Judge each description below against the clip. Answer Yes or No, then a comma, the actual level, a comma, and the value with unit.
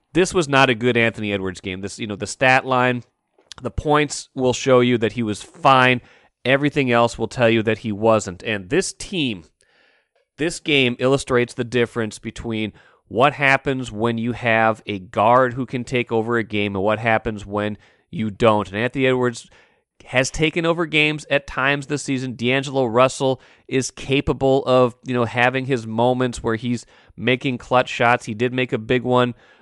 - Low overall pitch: Yes, low, 125 Hz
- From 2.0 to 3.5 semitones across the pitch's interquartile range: Yes, average, 2.8 semitones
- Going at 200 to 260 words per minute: No, average, 185 wpm